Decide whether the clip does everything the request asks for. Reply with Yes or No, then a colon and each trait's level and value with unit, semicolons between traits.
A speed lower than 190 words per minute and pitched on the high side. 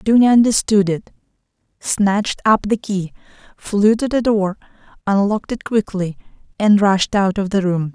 Yes: average, 150 wpm; high, 205 Hz